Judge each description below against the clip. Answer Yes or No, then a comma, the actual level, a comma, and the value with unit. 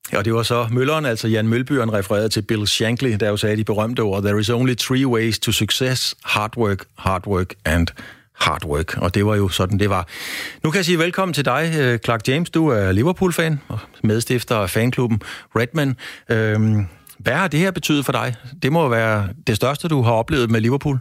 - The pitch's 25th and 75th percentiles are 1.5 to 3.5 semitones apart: No, average, 4.2 semitones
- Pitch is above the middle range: No, low, 115 Hz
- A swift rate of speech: No, average, 210 wpm